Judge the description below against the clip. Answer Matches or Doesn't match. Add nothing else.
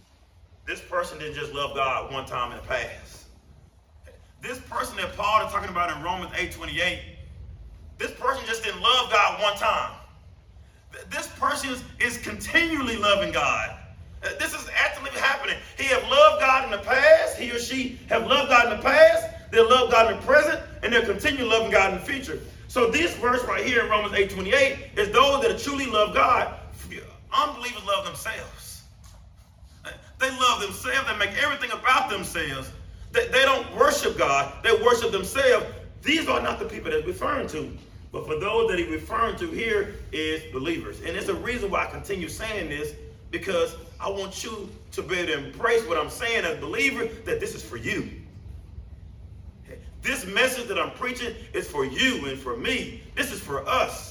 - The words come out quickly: Doesn't match